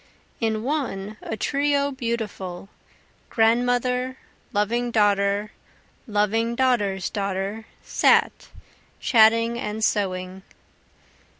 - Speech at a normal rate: No, slow, 80 wpm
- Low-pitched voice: No, high, 220 Hz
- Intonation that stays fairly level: No, average, 3.2 semitones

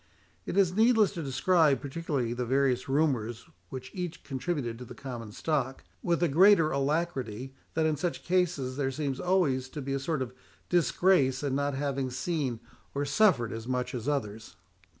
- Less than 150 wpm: No, average, 170 wpm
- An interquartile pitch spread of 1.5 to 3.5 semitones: No, average, 4.6 semitones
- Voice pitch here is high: No, medium, 140 Hz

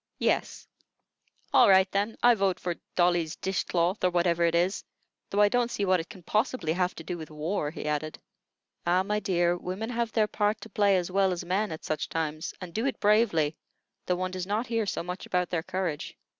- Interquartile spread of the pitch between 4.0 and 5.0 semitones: No, average, 3.3 semitones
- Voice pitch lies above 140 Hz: Yes, medium, 185 Hz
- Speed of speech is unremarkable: No, fast, 215 wpm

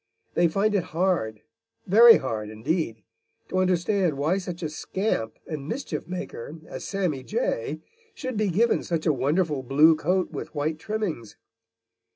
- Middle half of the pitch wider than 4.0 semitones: Yes, average, 5.1 semitones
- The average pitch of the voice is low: No, medium, 170 Hz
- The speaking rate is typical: Yes, average, 145 wpm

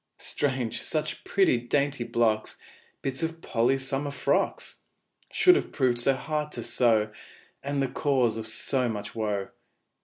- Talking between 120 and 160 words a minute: Yes, average, 145 wpm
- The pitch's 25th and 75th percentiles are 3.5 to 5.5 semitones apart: Yes, average, 3.8 semitones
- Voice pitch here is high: No, low, 130 Hz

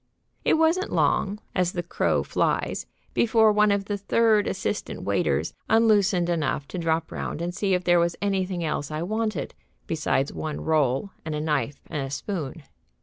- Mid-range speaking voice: Yes, medium, 175 Hz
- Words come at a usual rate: Yes, average, 165 wpm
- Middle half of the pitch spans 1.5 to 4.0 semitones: No, average, 4.8 semitones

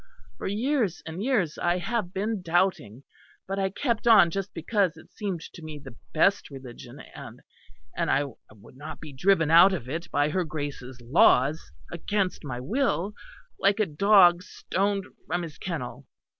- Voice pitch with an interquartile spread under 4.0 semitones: No, average, 5.1 semitones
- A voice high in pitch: No, medium, 175 Hz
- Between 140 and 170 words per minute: Yes, average, 165 wpm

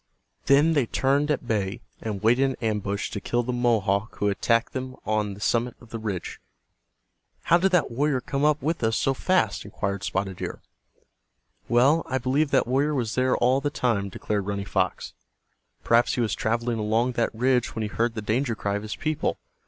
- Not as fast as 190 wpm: No, average, 200 wpm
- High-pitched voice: No, low, 120 Hz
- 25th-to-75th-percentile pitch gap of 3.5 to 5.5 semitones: Yes, average, 3.9 semitones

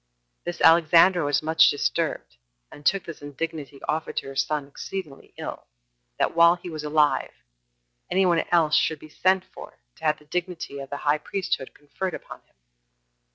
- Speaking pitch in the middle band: Yes, medium, 155 Hz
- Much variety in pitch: No, average, 3.1 semitones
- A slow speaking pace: No, average, 170 wpm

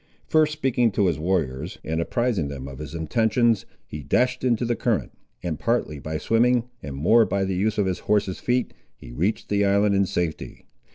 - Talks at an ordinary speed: Yes, average, 190 wpm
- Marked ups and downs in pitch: Yes, wide, 6.6 semitones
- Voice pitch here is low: Yes, low, 100 Hz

